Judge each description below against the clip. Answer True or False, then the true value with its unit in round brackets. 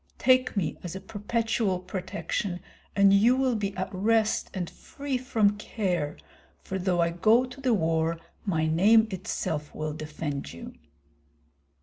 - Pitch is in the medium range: False (195 Hz)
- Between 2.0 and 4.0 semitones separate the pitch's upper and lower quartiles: False (4.8 semitones)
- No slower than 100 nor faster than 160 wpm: True (145 wpm)